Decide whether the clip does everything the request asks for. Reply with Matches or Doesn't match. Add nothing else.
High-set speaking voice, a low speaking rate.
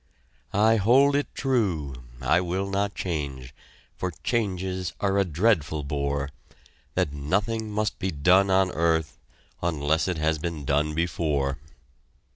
Doesn't match